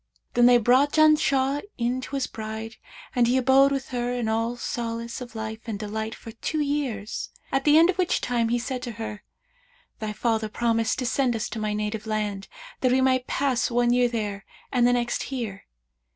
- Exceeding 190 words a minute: Yes, average, 200 wpm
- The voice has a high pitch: Yes, high, 240 Hz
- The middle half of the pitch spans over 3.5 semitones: No, average, 2.9 semitones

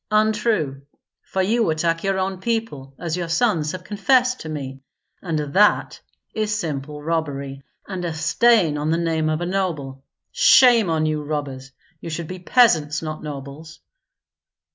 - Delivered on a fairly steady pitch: No, average, 4.8 semitones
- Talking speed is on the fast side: No, average, 155 wpm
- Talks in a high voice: No, medium, 165 Hz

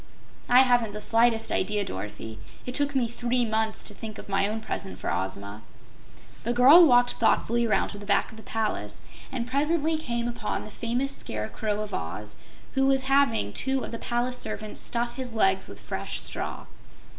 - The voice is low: No, high, 230 Hz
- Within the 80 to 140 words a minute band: No, average, 185 wpm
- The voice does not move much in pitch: No, average, 3.4 semitones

